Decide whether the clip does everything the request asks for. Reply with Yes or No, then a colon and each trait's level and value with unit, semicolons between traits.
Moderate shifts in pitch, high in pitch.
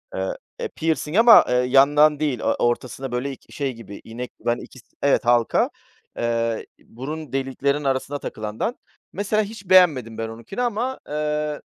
No: average, 4.7 semitones; medium, 140 Hz